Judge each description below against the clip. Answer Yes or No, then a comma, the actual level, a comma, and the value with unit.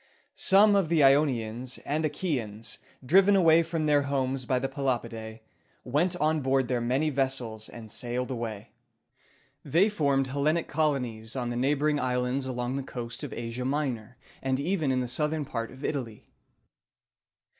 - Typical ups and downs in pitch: Yes, average, 3.8 semitones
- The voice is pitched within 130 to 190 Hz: Yes, low, 135 Hz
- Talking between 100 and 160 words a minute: Yes, average, 155 wpm